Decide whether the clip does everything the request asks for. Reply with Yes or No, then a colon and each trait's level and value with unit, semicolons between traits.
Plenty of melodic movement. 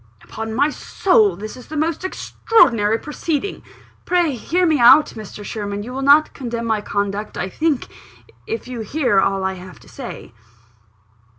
Yes: wide, 6.7 semitones